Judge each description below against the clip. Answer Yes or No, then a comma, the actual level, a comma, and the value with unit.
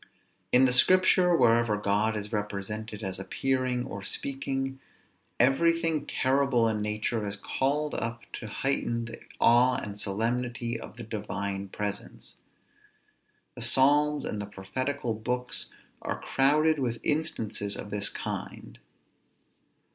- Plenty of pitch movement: No, average, 4.4 semitones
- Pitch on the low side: Yes, low, 120 Hz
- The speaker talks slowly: Yes, slow, 125 wpm